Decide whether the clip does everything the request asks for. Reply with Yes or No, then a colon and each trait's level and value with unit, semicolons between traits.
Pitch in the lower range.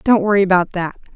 No: high, 190 Hz